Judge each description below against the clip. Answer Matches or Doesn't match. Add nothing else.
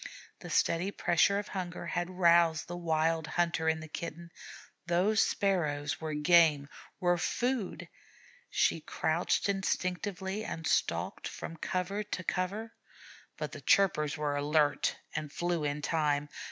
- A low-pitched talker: Doesn't match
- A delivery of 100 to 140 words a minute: Matches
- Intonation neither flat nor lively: Matches